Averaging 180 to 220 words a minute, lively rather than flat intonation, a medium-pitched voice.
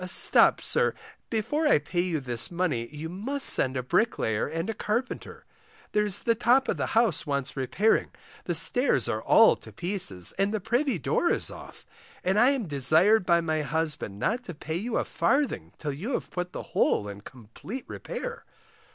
Yes: average, 185 wpm; wide, 7.4 semitones; medium, 180 Hz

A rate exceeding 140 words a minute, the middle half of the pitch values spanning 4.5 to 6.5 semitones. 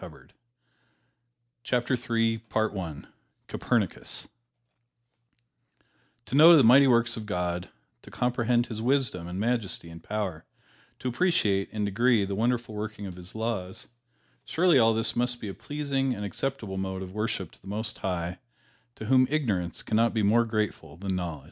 No: average, 150 wpm; average, 4.1 semitones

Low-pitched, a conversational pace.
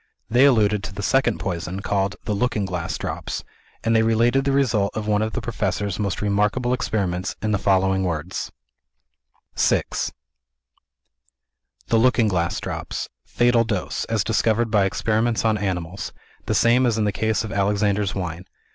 Yes: low, 105 Hz; average, 160 wpm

